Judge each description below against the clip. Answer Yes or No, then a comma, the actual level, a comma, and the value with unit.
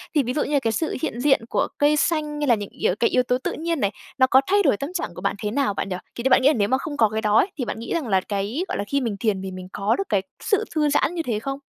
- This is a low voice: No, very high, 255 Hz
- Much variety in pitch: Yes, wide, 6.1 semitones